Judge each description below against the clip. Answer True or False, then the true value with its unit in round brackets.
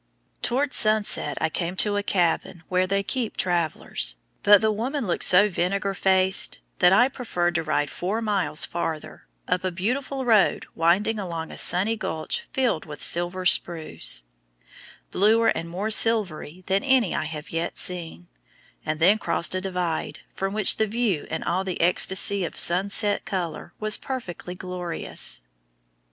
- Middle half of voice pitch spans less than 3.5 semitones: False (3.8 semitones)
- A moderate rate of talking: True (155 wpm)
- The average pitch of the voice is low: False (185 Hz)